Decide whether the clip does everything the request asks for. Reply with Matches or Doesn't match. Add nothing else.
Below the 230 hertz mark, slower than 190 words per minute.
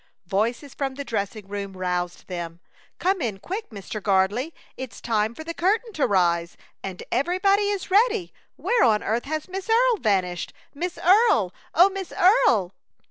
Doesn't match